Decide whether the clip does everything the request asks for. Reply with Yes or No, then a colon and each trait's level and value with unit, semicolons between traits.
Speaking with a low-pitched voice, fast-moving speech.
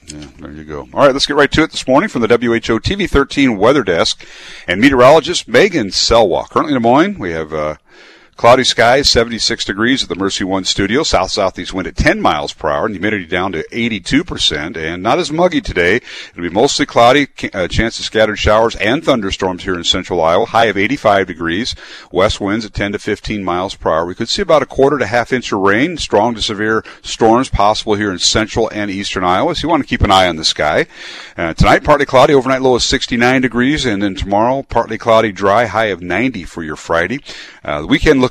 Yes: low, 110 Hz; fast, 220 wpm